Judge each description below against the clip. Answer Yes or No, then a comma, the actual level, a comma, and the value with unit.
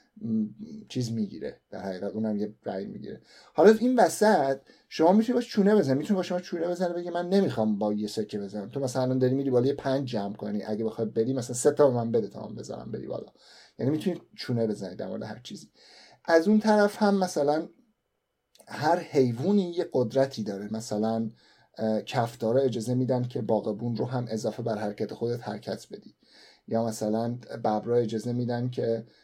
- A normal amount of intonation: No, wide, 7.7 semitones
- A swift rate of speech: Yes, fast, 185 wpm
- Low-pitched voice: Yes, low, 125 Hz